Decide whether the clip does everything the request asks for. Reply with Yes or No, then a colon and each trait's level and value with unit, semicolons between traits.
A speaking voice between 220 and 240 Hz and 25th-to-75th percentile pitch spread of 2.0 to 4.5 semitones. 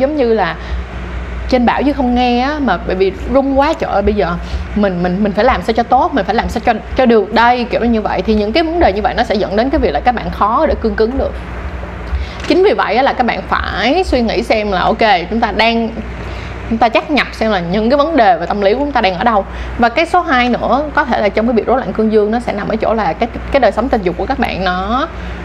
Yes: high, 230 Hz; average, 4.2 semitones